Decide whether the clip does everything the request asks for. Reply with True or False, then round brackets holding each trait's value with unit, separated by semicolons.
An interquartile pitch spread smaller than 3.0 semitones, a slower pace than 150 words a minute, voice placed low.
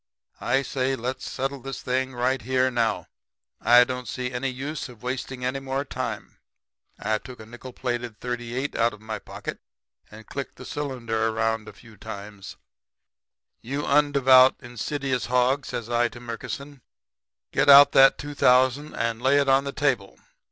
False (2.4 semitones; 165 wpm; 125 Hz)